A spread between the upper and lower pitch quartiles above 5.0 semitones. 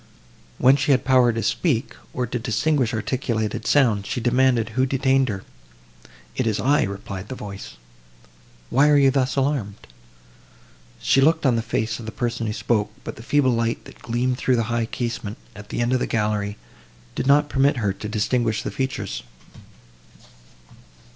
No: average, 3.7 semitones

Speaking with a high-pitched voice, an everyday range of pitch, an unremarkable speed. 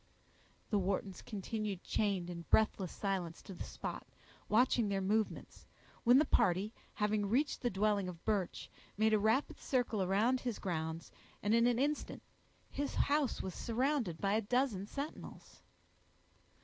Yes: high, 210 Hz; average, 4.1 semitones; average, 150 wpm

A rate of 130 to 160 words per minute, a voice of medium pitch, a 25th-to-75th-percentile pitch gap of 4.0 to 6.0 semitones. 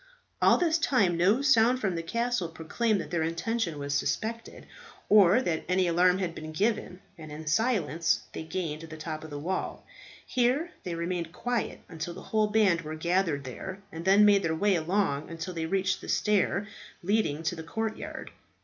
No: average, 185 wpm; medium, 180 Hz; average, 4.7 semitones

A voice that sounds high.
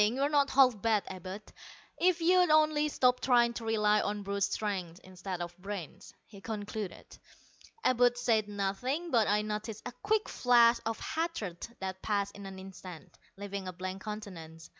Yes: high, 210 Hz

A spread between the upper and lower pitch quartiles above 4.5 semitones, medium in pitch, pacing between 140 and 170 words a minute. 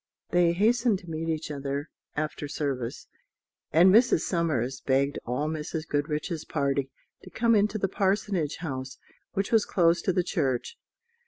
Yes: average, 5.1 semitones; medium, 160 Hz; average, 150 wpm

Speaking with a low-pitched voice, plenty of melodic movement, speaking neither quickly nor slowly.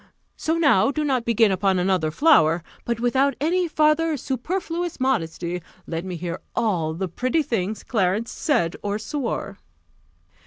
No: high, 230 Hz; wide, 8.4 semitones; average, 145 wpm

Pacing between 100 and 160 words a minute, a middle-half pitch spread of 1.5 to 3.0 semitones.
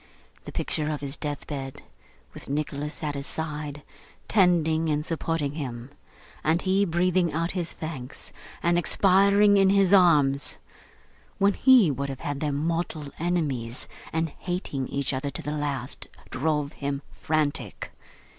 No: average, 140 wpm; average, 3.6 semitones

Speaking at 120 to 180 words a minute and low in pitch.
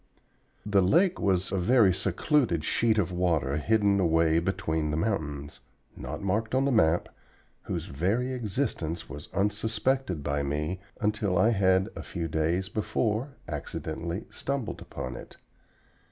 Yes: average, 140 wpm; very low, 95 Hz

